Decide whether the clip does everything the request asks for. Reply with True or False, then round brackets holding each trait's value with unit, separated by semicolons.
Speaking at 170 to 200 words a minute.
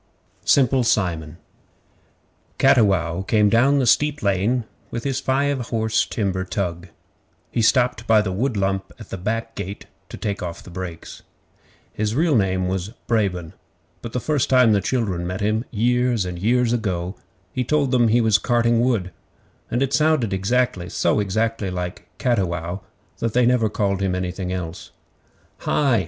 False (155 wpm)